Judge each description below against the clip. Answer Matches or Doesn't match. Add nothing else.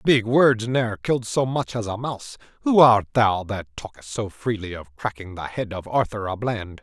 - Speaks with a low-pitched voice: Matches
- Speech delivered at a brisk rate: Matches